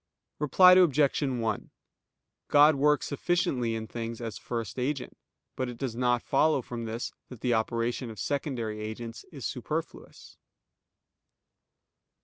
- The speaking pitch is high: No, low, 125 Hz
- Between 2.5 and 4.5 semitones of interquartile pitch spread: Yes, average, 3.8 semitones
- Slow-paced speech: Yes, slow, 125 wpm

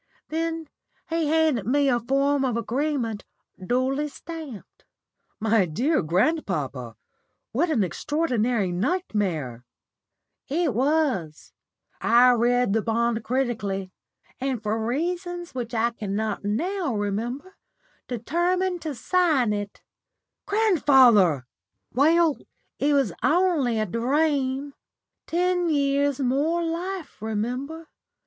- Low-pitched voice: No, very high, 260 Hz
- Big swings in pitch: Yes, wide, 6.4 semitones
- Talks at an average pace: No, slow, 100 wpm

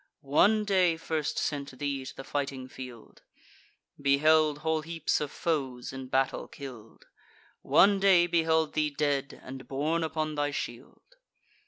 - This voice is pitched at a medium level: Yes, medium, 145 Hz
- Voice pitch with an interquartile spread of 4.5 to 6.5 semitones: No, average, 3.1 semitones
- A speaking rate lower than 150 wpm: Yes, average, 140 wpm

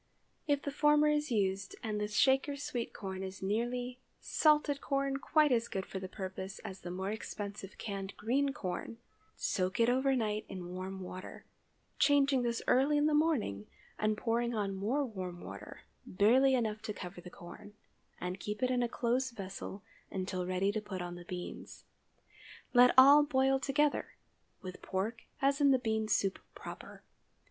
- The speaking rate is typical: Yes, average, 160 wpm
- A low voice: No, high, 220 Hz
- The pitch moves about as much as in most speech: No, wide, 5.8 semitones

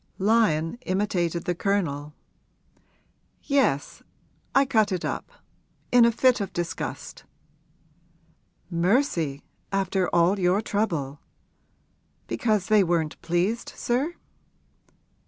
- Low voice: No, high, 190 Hz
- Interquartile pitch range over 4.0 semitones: Yes, average, 4.7 semitones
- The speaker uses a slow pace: Yes, slow, 95 wpm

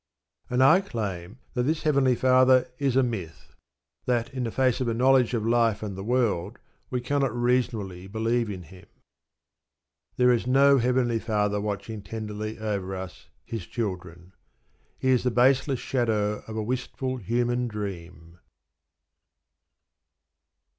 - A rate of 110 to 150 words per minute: Yes, average, 140 wpm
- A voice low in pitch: Yes, low, 115 Hz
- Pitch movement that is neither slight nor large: Yes, average, 3.7 semitones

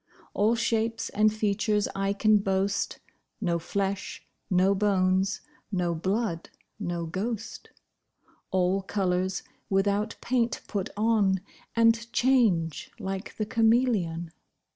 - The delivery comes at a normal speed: No, slow, 105 wpm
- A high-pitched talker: Yes, high, 200 Hz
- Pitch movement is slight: No, average, 3.0 semitones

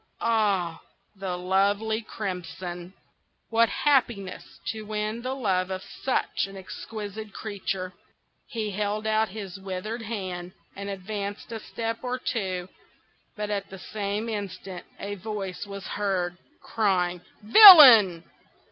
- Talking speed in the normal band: No, slow, 120 wpm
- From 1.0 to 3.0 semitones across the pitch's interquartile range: Yes, average, 2.7 semitones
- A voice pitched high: Yes, high, 200 Hz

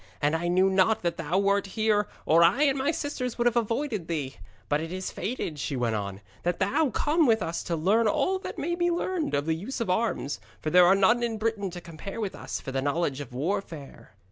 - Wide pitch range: Yes, wide, 6.3 semitones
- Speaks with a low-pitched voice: No, high, 190 Hz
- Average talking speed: No, fast, 235 wpm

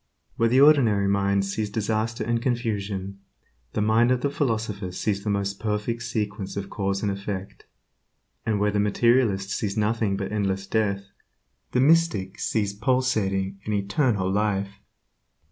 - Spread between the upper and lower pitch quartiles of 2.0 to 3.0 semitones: Yes, average, 2.7 semitones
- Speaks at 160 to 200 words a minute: No, average, 145 wpm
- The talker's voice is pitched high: No, low, 105 Hz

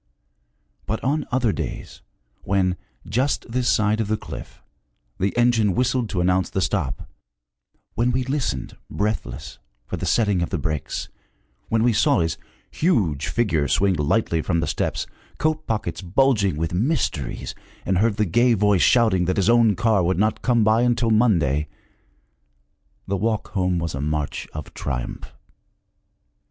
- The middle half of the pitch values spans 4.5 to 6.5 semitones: Yes, wide, 5.4 semitones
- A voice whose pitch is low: Yes, low, 105 Hz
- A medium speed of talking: Yes, average, 155 wpm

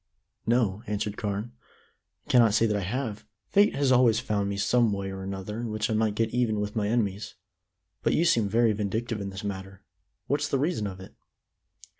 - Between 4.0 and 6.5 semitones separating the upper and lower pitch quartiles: No, average, 2.9 semitones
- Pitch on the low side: Yes, low, 105 Hz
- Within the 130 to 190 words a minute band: No, average, 200 wpm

